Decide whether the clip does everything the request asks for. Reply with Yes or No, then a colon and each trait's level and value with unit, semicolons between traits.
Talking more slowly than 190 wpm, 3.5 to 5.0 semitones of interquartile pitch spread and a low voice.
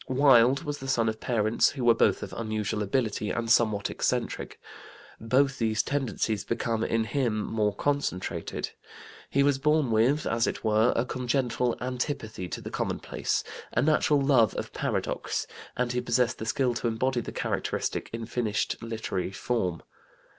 No: average, 160 wpm; average, 3.1 semitones; low, 115 Hz